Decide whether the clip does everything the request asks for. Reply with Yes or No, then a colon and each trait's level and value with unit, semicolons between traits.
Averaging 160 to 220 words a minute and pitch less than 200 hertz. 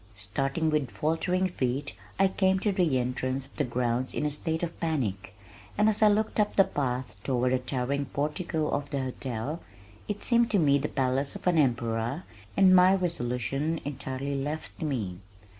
Yes: average, 175 wpm; medium, 140 Hz